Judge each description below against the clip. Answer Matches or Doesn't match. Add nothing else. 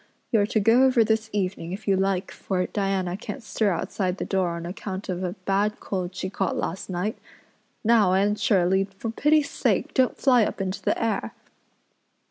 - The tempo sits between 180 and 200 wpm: Matches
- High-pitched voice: Matches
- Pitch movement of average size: Matches